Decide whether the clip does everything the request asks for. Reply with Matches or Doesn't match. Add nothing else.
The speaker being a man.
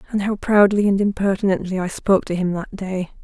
Doesn't match